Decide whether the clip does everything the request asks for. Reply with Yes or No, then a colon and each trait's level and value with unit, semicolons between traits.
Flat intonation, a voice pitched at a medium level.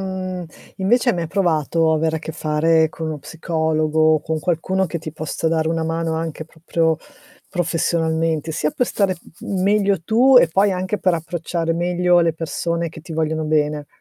Yes: narrow, 2.2 semitones; medium, 165 Hz